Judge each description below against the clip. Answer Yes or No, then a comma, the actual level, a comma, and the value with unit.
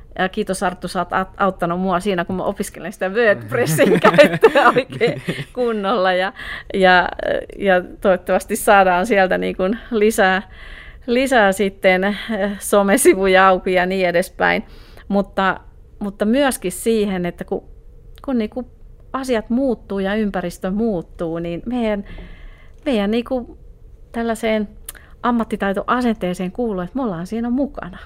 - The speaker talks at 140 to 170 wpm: No, average, 125 wpm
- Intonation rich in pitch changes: No, average, 3.6 semitones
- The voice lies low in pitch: No, high, 200 Hz